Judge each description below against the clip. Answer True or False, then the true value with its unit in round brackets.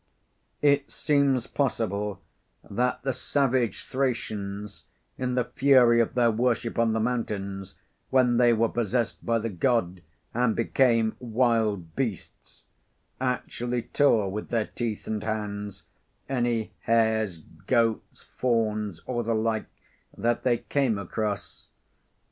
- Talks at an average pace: False (120 wpm)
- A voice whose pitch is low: True (115 Hz)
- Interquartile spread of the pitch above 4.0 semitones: False (2.7 semitones)